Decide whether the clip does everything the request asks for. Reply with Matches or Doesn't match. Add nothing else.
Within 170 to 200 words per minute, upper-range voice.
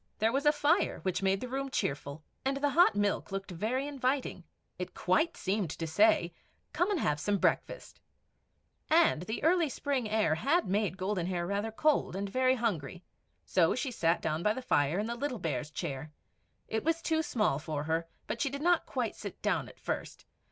Matches